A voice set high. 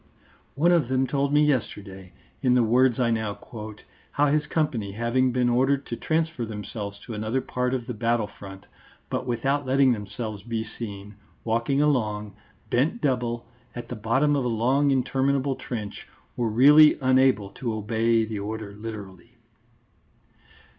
No: low, 120 Hz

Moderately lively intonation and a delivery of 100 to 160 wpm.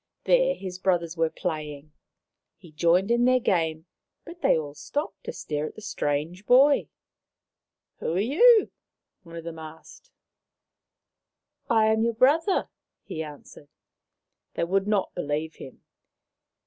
No: wide, 7.0 semitones; average, 150 wpm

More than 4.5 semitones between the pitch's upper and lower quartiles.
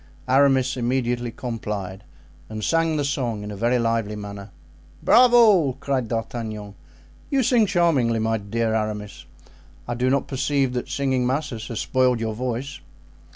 No: average, 3.8 semitones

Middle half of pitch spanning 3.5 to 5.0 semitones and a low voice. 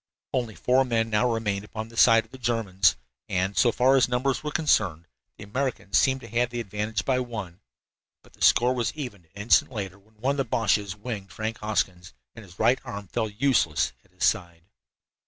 Yes: average, 3.8 semitones; low, 110 Hz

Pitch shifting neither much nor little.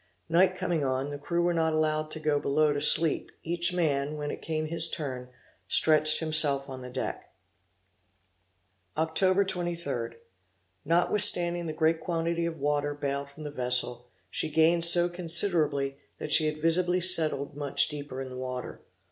Yes: average, 3.0 semitones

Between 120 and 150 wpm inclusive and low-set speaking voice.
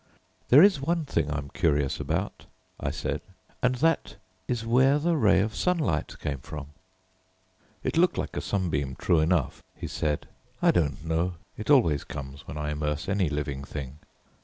No: average, 165 wpm; very low, 80 Hz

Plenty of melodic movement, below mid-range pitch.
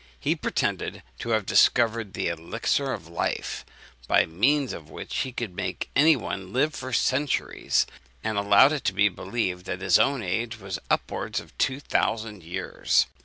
Yes: wide, 5.7 semitones; low, 110 Hz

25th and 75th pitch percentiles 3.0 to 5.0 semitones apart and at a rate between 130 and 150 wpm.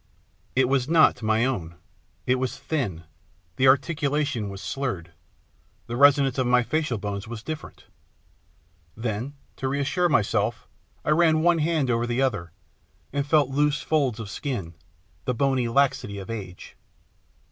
Yes: average, 4.4 semitones; average, 145 wpm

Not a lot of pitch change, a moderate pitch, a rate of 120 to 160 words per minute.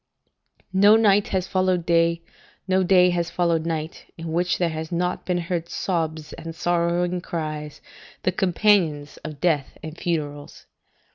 Yes: narrow, 2.1 semitones; medium, 170 Hz; average, 145 wpm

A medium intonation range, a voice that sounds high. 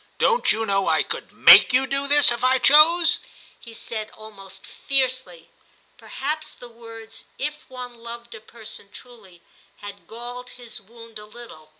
Yes: average, 3.0 semitones; high, 235 Hz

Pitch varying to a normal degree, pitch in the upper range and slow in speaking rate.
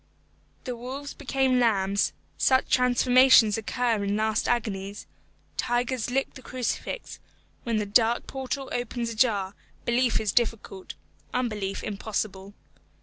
Yes: average, 3.3 semitones; high, 235 Hz; slow, 115 wpm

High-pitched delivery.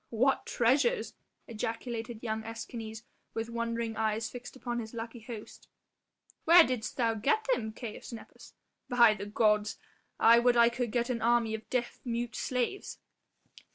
Yes: high, 235 Hz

